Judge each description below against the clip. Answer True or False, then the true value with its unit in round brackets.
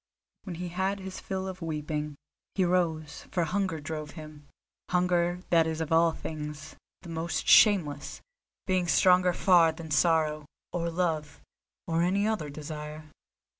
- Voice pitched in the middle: True (165 Hz)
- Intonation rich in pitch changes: False (2.9 semitones)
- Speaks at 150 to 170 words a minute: False (140 wpm)